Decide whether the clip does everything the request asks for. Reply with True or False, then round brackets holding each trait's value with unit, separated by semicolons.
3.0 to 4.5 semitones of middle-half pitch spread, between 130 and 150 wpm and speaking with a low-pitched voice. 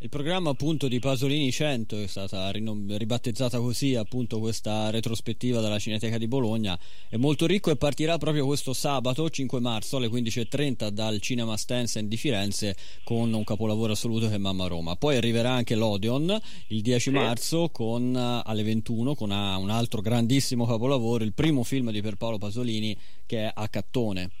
False (3.6 semitones; 170 wpm; 115 Hz)